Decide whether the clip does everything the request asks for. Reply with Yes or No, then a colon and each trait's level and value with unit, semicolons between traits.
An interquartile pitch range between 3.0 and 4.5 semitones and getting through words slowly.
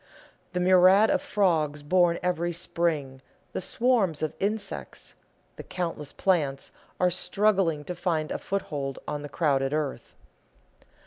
Yes: average, 3.9 semitones; slow, 130 wpm